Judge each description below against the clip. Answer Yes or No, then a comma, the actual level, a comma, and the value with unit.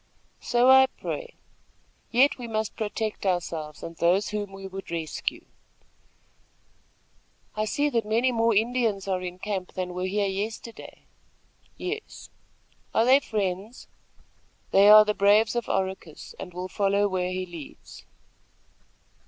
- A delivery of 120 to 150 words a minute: Yes, slow, 135 wpm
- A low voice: No, high, 205 Hz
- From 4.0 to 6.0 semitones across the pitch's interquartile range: No, average, 3.5 semitones